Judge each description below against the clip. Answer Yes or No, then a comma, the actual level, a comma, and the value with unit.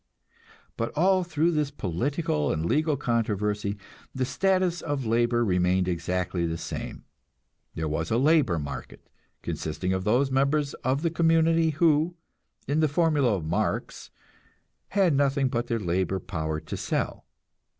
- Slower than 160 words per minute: Yes, average, 140 wpm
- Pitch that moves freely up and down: Yes, wide, 9.0 semitones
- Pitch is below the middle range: Yes, low, 125 Hz